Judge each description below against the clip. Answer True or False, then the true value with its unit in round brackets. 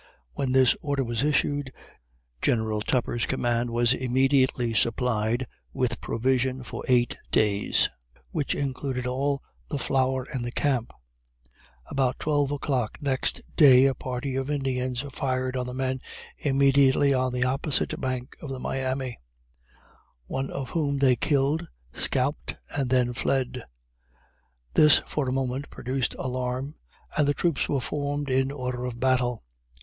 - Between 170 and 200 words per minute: False (135 wpm)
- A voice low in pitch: True (130 Hz)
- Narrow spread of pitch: True (1.7 semitones)